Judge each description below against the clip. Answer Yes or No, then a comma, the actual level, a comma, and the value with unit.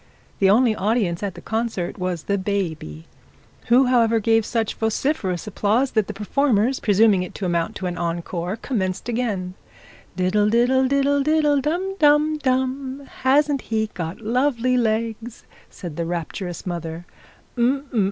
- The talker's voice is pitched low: No, high, 220 Hz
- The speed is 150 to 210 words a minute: No, average, 140 wpm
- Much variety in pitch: Yes, wide, 5.9 semitones